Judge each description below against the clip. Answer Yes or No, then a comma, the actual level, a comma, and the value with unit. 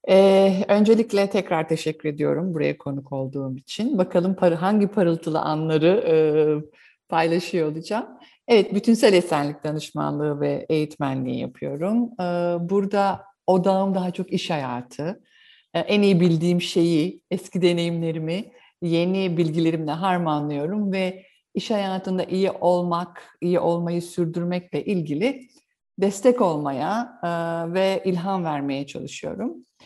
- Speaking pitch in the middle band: Yes, medium, 175 Hz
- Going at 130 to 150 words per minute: No, average, 115 wpm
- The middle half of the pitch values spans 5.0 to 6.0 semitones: No, average, 3.6 semitones